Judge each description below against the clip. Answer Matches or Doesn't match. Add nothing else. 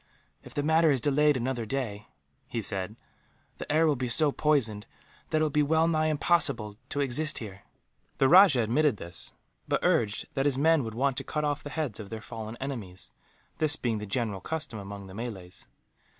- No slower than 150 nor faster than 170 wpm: Doesn't match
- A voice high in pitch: Doesn't match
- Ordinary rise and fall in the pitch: Doesn't match